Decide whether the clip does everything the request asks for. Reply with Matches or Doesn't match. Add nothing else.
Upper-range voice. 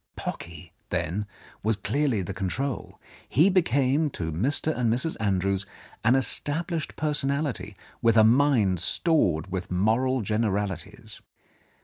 Doesn't match